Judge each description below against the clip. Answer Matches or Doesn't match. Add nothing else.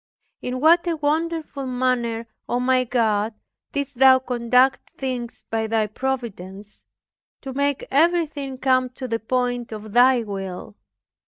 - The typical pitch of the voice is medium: Doesn't match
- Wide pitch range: Doesn't match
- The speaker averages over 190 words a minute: Doesn't match